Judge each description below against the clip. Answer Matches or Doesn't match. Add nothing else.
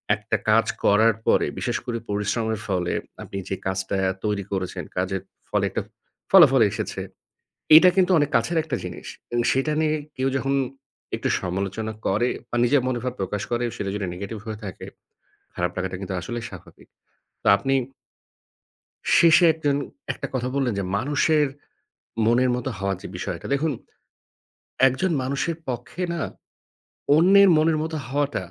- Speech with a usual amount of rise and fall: Doesn't match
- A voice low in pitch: Matches